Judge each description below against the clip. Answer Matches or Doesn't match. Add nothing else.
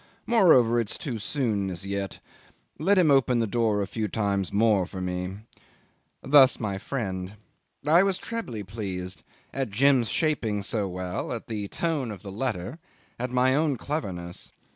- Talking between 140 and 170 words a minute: Matches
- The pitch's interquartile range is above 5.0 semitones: Matches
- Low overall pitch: Matches